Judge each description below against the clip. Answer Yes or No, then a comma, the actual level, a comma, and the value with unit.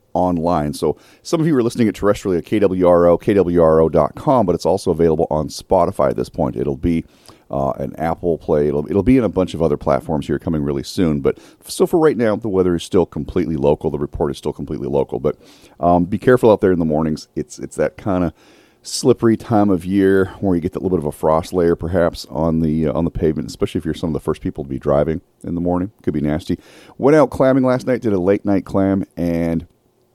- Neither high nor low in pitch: No, very low, 85 Hz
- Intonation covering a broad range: No, average, 3.8 semitones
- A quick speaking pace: Yes, fast, 240 wpm